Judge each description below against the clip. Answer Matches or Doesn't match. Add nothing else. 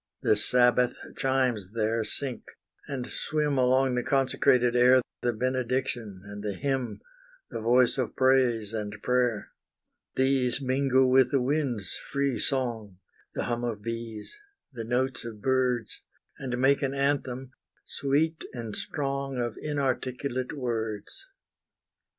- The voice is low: Matches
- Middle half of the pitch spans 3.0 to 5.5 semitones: Doesn't match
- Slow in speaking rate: Matches